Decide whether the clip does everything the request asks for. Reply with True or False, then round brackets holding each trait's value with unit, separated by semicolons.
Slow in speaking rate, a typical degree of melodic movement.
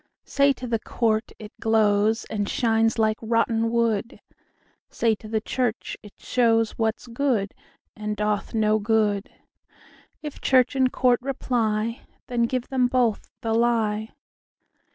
False (115 wpm; 2.1 semitones)